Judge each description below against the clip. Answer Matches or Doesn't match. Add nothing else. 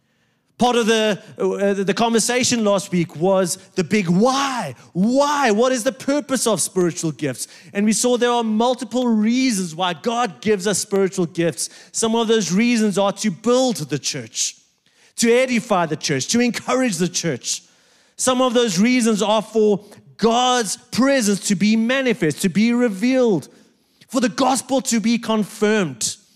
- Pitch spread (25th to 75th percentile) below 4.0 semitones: Doesn't match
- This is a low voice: Doesn't match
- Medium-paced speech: Matches